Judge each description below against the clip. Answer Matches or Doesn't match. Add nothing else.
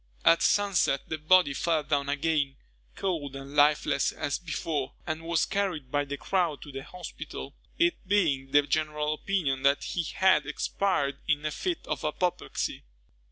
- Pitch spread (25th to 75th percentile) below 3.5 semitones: Doesn't match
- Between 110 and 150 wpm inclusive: Doesn't match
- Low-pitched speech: Doesn't match